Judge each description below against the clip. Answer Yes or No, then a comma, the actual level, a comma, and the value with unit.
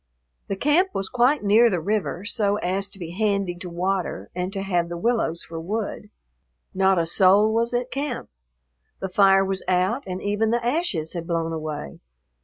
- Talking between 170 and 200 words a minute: Yes, average, 185 wpm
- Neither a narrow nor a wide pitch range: Yes, average, 3.9 semitones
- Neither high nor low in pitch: No, high, 195 Hz